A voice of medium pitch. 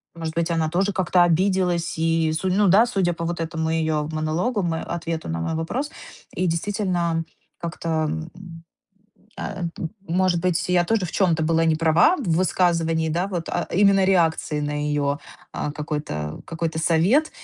Yes: medium, 165 Hz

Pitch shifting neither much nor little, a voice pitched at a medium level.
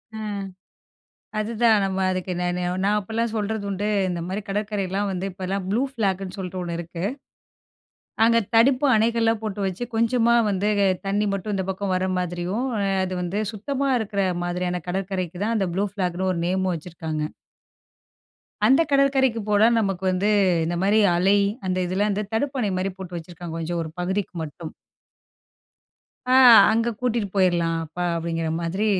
No: average, 3.3 semitones; high, 195 Hz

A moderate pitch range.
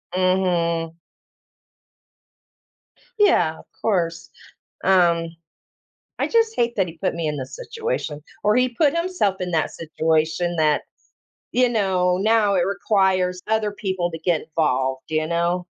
Yes: average, 4.2 semitones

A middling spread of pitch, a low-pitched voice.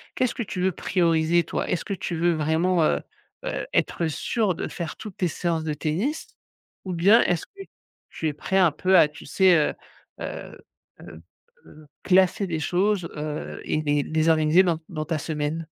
No: average, 3.1 semitones; medium, 170 Hz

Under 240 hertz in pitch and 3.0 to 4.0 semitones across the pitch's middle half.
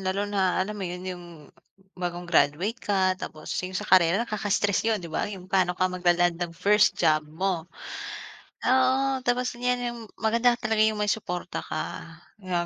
Yes: high, 190 Hz; average, 3.6 semitones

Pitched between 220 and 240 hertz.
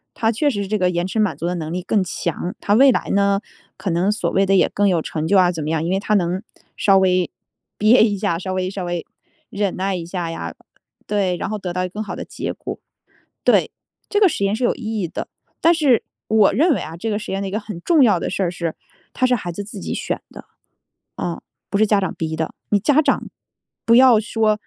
No: high, 195 Hz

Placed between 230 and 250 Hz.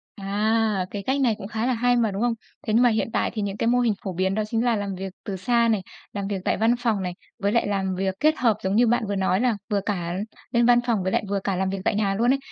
No: high, 210 Hz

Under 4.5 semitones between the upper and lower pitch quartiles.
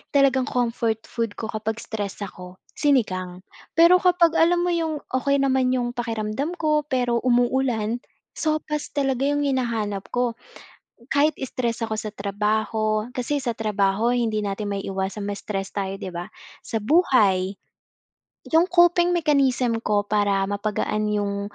No: average, 5.3 semitones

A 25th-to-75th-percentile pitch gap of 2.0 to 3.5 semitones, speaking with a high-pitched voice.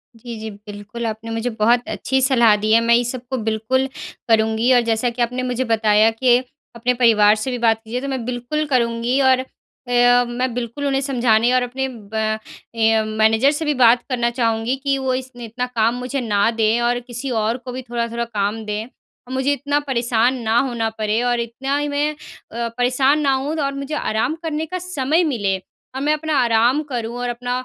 Yes: average, 2.8 semitones; high, 240 Hz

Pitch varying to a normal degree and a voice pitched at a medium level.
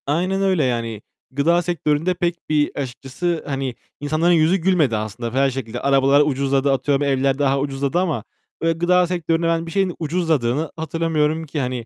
Yes: average, 3.7 semitones; medium, 150 Hz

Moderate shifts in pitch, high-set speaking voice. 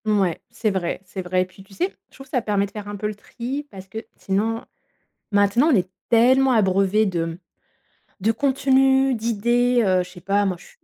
Yes: average, 4.2 semitones; high, 210 Hz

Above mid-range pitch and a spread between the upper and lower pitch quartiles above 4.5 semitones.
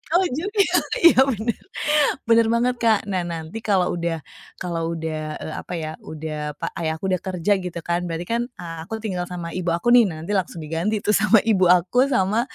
No: medium, 180 Hz; average, 4.9 semitones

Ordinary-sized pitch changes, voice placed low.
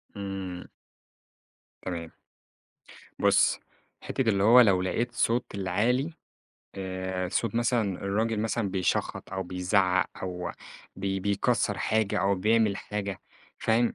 Yes: average, 3.2 semitones; low, 100 Hz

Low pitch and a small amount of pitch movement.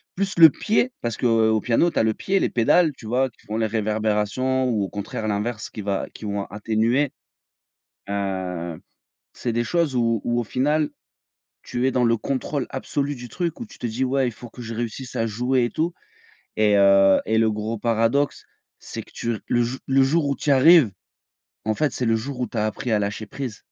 No: low, 120 Hz; average, 3.6 semitones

